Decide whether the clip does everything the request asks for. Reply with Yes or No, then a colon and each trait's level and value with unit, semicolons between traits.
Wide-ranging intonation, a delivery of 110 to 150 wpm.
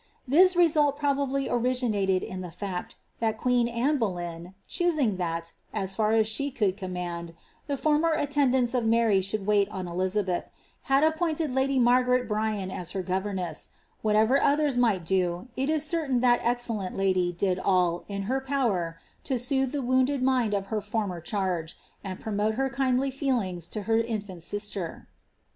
No: wide, 5.9 semitones; average, 165 wpm